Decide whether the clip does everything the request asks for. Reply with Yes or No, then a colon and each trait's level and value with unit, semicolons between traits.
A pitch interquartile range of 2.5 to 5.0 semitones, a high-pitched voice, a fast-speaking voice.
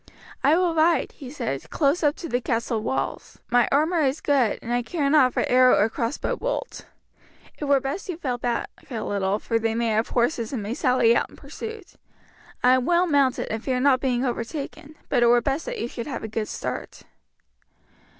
Yes: average, 4.1 semitones; very high, 255 Hz; fast, 210 wpm